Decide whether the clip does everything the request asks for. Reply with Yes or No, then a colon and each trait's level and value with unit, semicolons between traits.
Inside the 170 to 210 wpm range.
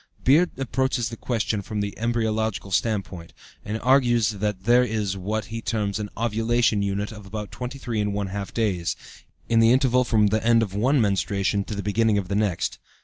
Yes: average, 175 wpm